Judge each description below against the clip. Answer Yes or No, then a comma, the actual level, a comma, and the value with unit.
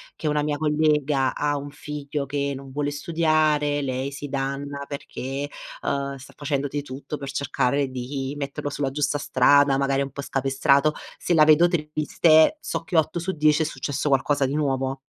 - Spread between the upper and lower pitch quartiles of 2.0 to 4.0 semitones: No, narrow, 1.6 semitones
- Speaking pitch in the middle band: Yes, medium, 145 Hz